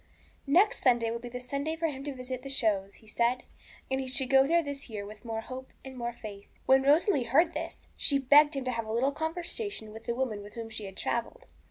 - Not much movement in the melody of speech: No, average, 3.7 semitones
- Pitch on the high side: Yes, very high, 255 Hz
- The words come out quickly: Yes, fast, 240 wpm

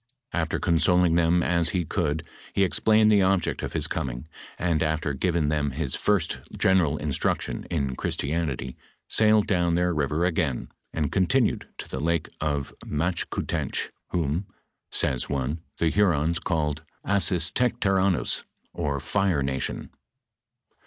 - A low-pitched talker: Yes, very low, 85 Hz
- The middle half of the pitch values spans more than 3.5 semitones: Yes, average, 3.9 semitones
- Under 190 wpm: Yes, slow, 135 wpm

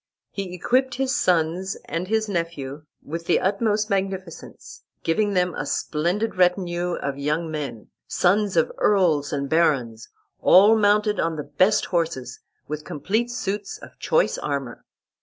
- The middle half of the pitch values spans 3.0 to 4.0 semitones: No, average, 5.2 semitones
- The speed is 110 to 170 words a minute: Yes, average, 140 wpm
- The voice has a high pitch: No, medium, 180 Hz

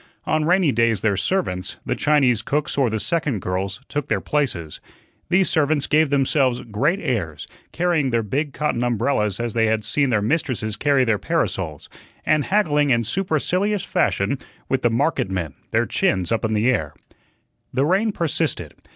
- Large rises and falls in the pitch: Yes, wide, 6.1 semitones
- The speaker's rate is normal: Yes, average, 165 wpm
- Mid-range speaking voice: No, low, 130 Hz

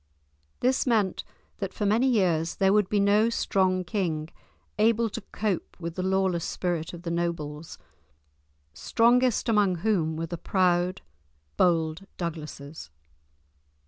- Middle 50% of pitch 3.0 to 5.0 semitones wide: Yes, average, 3.9 semitones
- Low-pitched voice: No, medium, 185 Hz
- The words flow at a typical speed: No, slow, 130 wpm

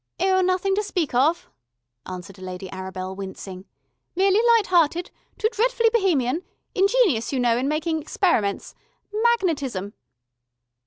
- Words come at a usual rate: No, slow, 115 wpm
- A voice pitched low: No, very high, 320 Hz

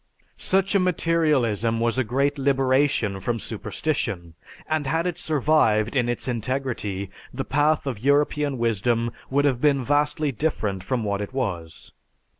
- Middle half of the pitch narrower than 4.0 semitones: No, average, 4.4 semitones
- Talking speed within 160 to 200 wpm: No, average, 145 wpm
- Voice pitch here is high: No, low, 130 Hz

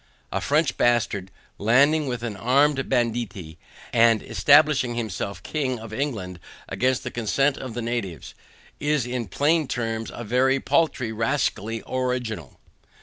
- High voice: No, low, 120 Hz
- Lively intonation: No, average, 3.4 semitones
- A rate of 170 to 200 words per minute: No, slow, 135 wpm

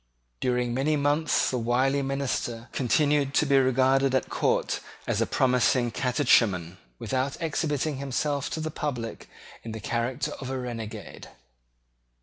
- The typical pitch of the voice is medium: No, low, 130 Hz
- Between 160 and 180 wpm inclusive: No, slow, 135 wpm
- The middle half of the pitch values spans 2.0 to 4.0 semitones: Yes, average, 2.8 semitones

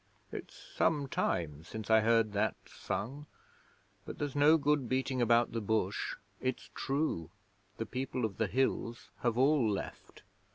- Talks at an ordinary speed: Yes, average, 150 wpm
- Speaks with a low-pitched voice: Yes, low, 120 Hz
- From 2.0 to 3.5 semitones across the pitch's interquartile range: No, average, 3.9 semitones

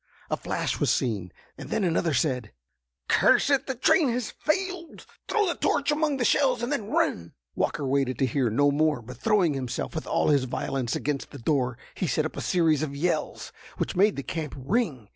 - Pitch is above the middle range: No, medium, 155 Hz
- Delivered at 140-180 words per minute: No, average, 200 wpm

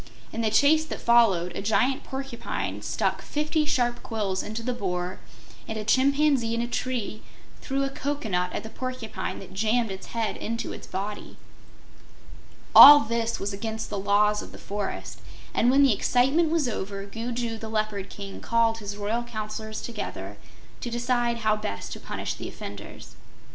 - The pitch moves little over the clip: No, average, 3.2 semitones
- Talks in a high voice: Yes, high, 225 Hz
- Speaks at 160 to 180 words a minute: Yes, average, 170 wpm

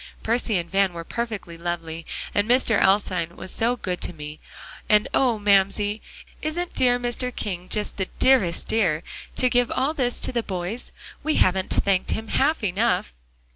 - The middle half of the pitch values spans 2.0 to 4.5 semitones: No, average, 5.2 semitones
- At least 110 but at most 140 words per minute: No, average, 170 wpm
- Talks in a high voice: Yes, high, 205 Hz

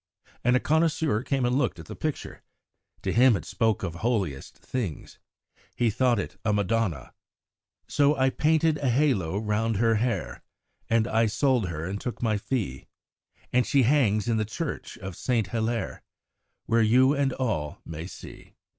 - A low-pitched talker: Yes, low, 115 Hz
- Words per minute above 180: No, average, 165 wpm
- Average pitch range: Yes, average, 4.1 semitones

